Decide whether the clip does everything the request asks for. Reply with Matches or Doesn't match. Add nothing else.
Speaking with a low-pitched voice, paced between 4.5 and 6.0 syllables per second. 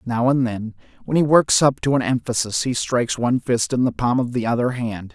Matches